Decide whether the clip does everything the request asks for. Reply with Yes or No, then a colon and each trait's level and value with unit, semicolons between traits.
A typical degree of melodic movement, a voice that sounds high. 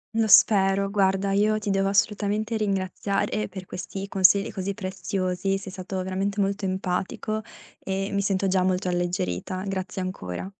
No: narrow, 1.2 semitones; high, 195 Hz